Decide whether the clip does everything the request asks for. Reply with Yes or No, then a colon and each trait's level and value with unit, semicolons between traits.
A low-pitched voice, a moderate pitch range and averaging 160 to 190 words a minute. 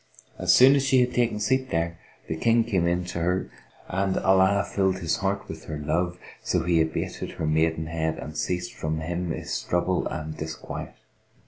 Yes: very low, 90 Hz; average, 3.6 semitones; average, 185 wpm